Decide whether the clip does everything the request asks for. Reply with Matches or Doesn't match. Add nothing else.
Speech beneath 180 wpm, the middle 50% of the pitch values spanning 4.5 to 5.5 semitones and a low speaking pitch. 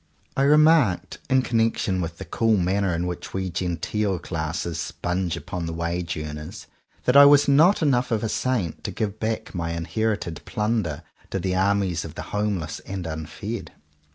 Matches